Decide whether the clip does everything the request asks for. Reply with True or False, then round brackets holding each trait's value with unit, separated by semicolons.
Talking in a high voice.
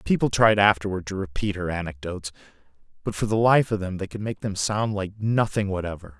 False (100 Hz)